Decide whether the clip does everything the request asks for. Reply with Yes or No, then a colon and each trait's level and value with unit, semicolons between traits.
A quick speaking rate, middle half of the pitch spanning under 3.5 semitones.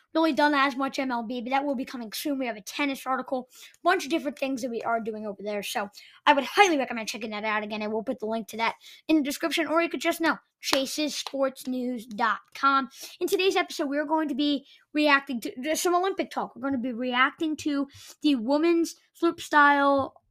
No: fast, 215 wpm; average, 4.1 semitones